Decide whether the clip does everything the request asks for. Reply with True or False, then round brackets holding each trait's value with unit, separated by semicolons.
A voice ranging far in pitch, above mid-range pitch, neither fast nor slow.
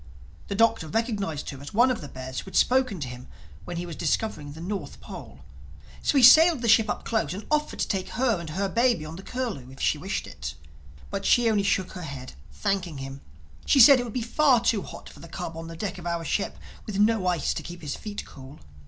False (6.2 semitones; 195 Hz; 245 wpm)